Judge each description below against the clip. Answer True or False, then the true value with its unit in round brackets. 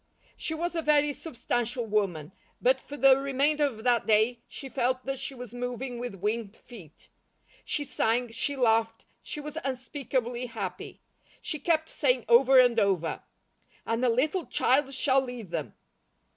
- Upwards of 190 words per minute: False (160 wpm)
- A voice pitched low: False (250 Hz)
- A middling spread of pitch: True (3.3 semitones)